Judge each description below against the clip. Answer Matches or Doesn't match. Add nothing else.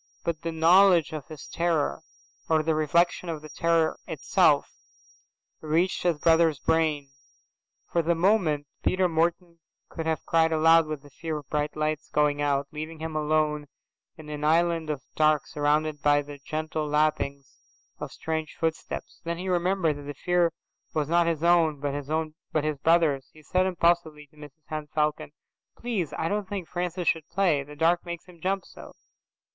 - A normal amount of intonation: Doesn't match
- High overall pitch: Doesn't match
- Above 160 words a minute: Matches